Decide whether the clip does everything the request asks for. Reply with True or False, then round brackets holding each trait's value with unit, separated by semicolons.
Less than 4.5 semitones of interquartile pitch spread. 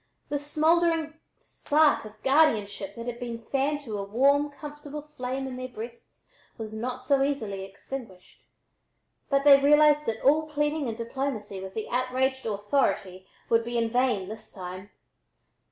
False (4.9 semitones)